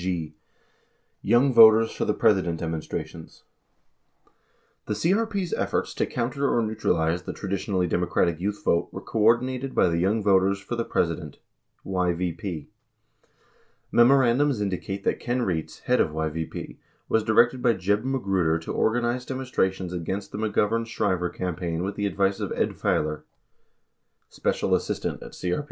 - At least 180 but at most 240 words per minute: No, average, 150 wpm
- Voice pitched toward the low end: Yes, low, 100 Hz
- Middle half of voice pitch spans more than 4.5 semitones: Yes, average, 5.1 semitones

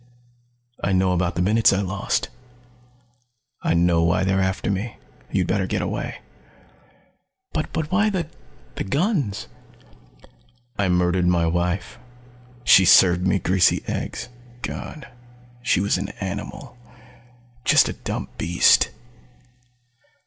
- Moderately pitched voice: No, very low, 95 Hz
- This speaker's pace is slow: Yes, slow, 120 wpm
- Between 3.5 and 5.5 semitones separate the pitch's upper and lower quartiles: No, average, 2.8 semitones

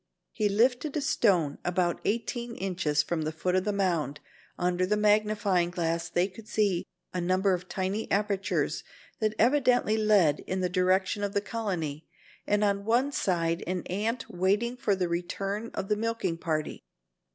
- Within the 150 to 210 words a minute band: Yes, average, 165 wpm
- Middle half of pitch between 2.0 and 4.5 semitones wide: Yes, average, 3.3 semitones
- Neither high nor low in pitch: No, high, 195 Hz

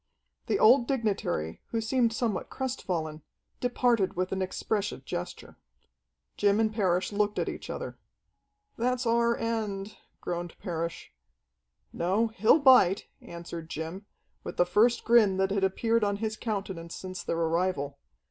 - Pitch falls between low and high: No, high, 200 Hz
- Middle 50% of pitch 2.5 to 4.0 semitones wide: No, average, 4.5 semitones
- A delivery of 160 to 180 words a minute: No, average, 140 wpm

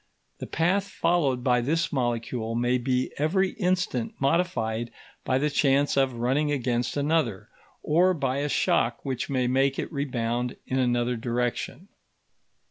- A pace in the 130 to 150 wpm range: Yes, average, 140 wpm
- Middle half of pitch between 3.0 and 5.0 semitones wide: Yes, average, 3.7 semitones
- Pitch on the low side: Yes, low, 130 Hz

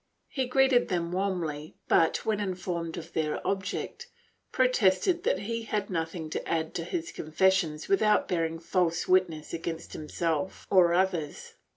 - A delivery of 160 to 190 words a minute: No, average, 145 wpm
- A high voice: No, medium, 180 Hz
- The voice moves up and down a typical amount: Yes, average, 3.5 semitones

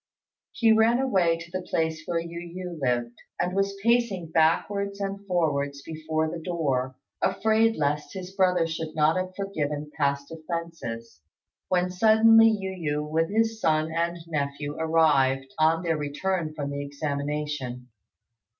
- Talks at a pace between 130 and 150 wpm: Yes, average, 145 wpm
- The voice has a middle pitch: Yes, medium, 165 Hz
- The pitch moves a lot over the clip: No, average, 4.1 semitones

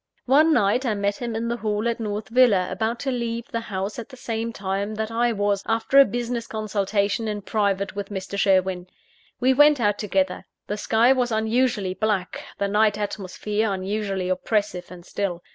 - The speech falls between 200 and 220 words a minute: No, average, 185 wpm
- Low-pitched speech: No, high, 210 Hz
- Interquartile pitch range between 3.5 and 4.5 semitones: No, average, 2.7 semitones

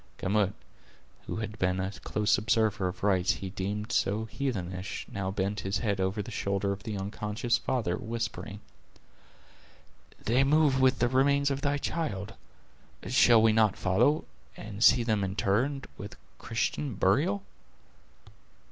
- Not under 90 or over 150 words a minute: Yes, average, 140 wpm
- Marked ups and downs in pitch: No, average, 3.7 semitones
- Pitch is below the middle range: Yes, low, 105 Hz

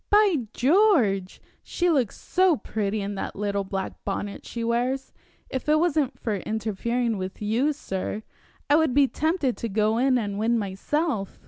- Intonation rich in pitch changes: Yes, wide, 6.1 semitones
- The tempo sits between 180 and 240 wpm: No, average, 160 wpm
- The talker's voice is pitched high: Yes, high, 235 Hz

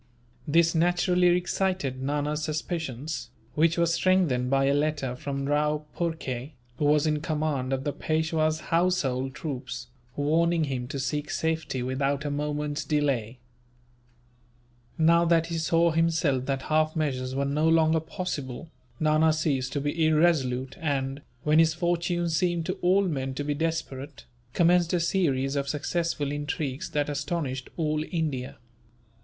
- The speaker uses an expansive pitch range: No, average, 3.2 semitones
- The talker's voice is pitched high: No, medium, 150 Hz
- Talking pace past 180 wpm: No, average, 140 wpm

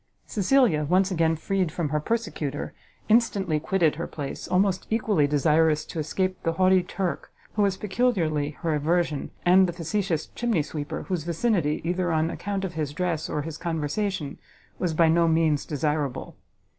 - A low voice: No, medium, 170 Hz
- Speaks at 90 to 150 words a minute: No, average, 160 wpm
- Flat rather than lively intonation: No, average, 3.7 semitones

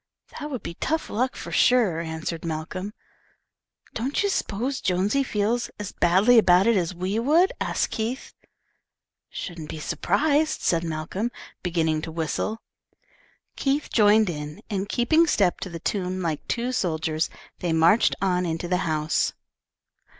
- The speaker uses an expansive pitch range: Yes, wide, 6.2 semitones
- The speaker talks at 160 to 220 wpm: No, average, 145 wpm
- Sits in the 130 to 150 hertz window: No, high, 190 Hz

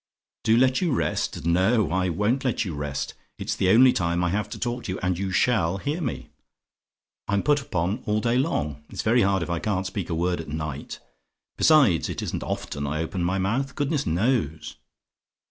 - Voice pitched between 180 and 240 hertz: No, very low, 95 Hz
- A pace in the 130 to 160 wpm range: No, average, 200 wpm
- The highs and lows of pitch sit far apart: Yes, wide, 6.3 semitones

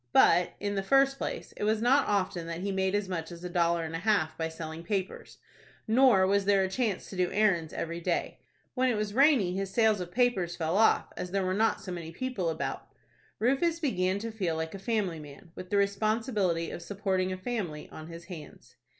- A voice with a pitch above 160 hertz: Yes, high, 190 Hz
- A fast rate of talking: Yes, fast, 220 wpm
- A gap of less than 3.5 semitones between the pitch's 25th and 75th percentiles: No, average, 4.1 semitones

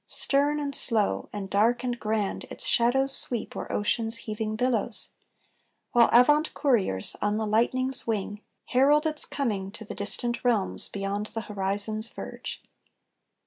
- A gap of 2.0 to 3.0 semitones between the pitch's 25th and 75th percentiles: No, average, 3.5 semitones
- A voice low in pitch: No, high, 225 Hz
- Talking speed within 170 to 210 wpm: No, average, 145 wpm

